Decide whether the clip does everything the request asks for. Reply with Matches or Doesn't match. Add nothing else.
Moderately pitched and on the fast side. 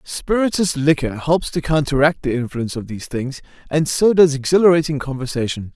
Doesn't match